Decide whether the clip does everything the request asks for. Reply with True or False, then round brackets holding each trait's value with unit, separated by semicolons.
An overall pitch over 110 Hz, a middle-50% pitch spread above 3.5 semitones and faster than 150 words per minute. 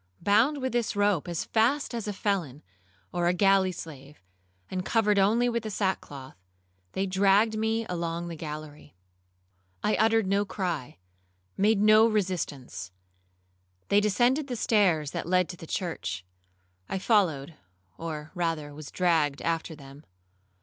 False (185 Hz; 5.3 semitones; 145 wpm)